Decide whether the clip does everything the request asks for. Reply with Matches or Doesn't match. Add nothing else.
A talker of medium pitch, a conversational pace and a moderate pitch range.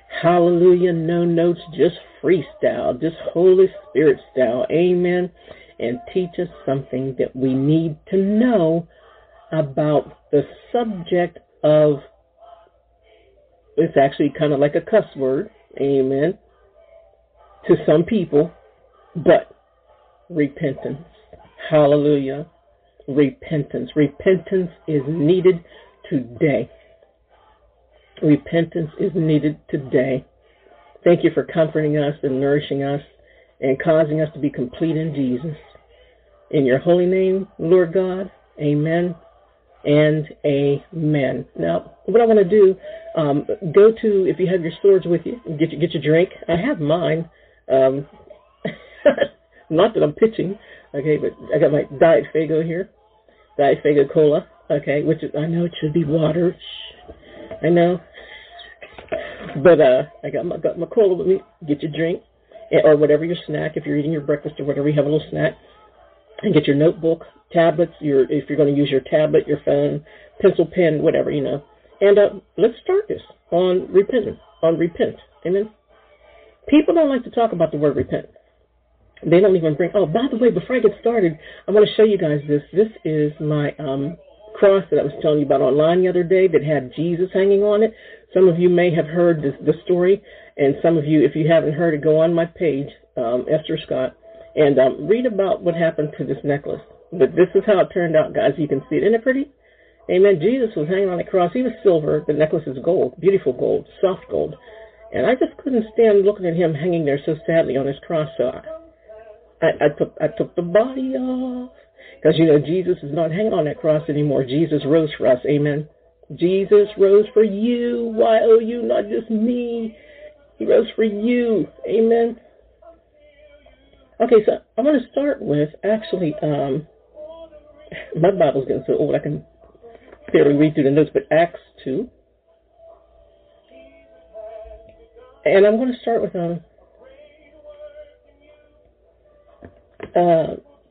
Doesn't match